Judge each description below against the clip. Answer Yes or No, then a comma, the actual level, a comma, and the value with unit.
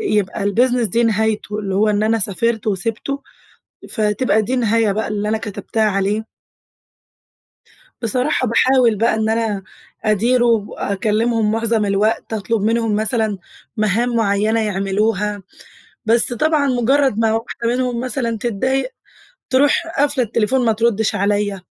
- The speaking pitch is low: No, high, 220 Hz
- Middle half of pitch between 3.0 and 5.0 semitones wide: No, narrow, 2.4 semitones